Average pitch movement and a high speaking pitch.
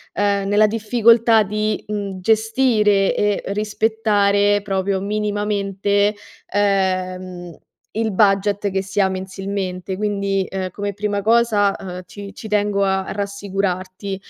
No: narrow, 1.5 semitones; high, 200 Hz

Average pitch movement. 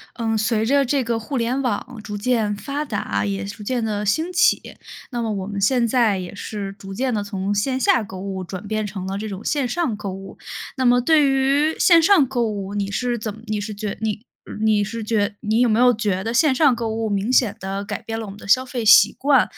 Yes: average, 3.7 semitones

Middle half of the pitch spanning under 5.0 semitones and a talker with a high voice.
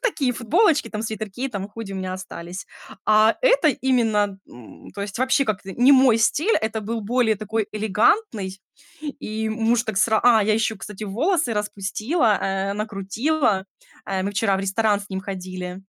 Yes: average, 3.6 semitones; high, 215 Hz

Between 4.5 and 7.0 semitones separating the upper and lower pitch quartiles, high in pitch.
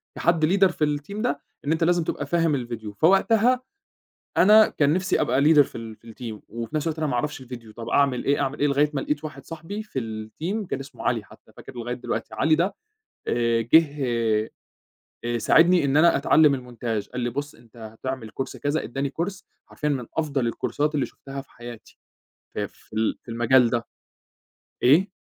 No: average, 5.0 semitones; medium, 140 Hz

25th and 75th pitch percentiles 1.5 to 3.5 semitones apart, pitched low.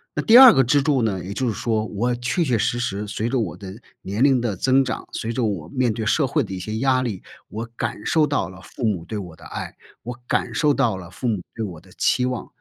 No: average, 4.4 semitones; low, 115 Hz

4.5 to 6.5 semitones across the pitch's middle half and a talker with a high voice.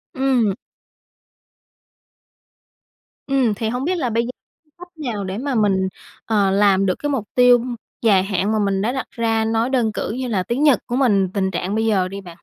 No: average, 4.1 semitones; high, 225 Hz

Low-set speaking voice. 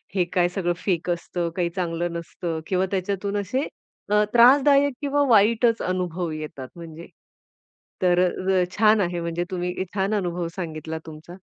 No: medium, 180 Hz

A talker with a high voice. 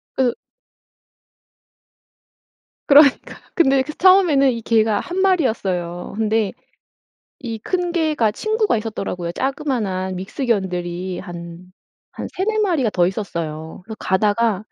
Yes: high, 225 Hz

